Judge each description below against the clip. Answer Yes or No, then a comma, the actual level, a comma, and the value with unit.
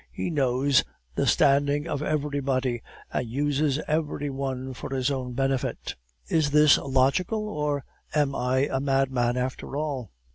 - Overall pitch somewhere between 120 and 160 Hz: Yes, medium, 140 Hz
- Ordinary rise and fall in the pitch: No, narrow, 2.0 semitones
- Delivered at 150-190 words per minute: No, average, 140 wpm